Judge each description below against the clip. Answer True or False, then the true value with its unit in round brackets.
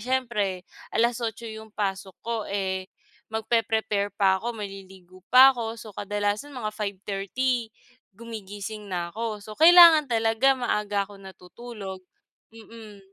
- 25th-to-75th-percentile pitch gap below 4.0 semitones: True (2.9 semitones)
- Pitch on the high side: True (215 Hz)